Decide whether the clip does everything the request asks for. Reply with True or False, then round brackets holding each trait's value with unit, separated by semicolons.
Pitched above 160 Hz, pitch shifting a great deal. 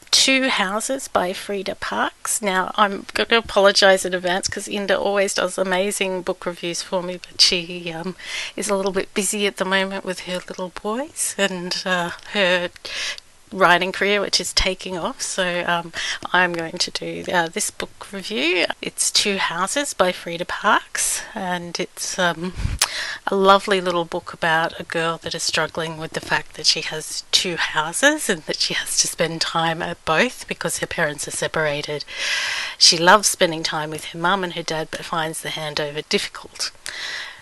False (185 Hz; 2.8 semitones)